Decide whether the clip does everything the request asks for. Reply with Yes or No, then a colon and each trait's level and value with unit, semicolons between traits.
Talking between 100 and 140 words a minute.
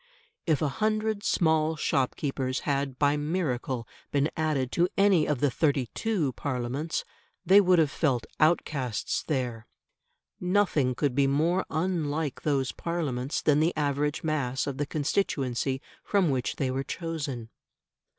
Yes: slow, 135 wpm